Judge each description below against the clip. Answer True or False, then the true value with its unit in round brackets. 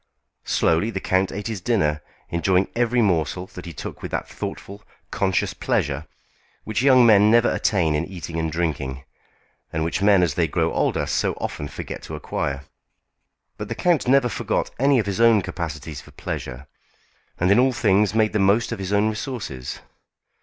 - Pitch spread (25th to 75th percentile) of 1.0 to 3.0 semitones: False (5.5 semitones)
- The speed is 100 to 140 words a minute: False (180 wpm)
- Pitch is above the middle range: False (95 Hz)